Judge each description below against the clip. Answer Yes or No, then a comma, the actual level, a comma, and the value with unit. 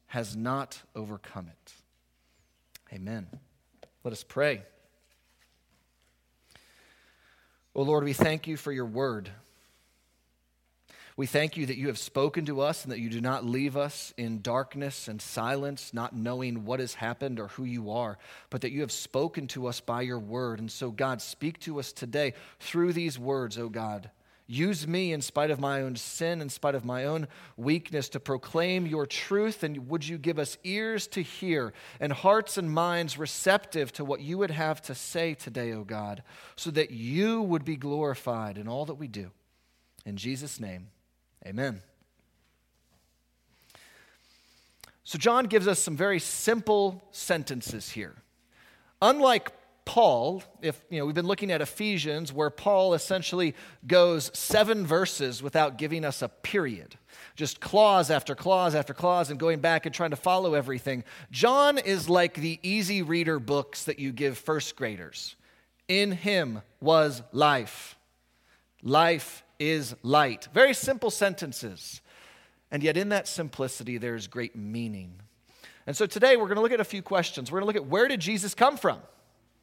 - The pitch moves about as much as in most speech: No, wide, 6.5 semitones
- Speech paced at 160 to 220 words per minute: Yes, average, 165 wpm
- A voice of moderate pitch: Yes, medium, 145 Hz